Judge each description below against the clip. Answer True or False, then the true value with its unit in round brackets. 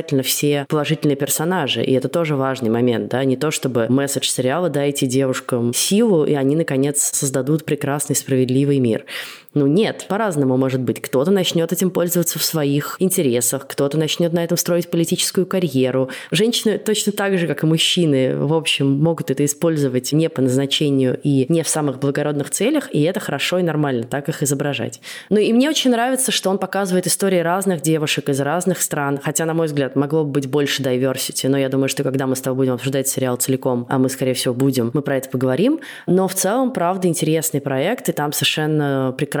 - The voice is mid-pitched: True (145 Hz)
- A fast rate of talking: True (190 wpm)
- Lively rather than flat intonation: False (4.3 semitones)